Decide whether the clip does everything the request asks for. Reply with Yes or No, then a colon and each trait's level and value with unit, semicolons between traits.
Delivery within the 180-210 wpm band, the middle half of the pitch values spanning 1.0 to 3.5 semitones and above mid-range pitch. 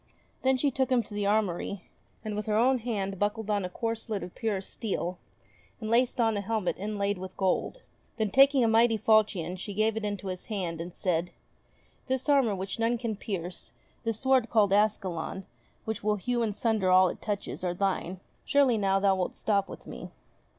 Yes: average, 195 wpm; average, 3.1 semitones; high, 210 Hz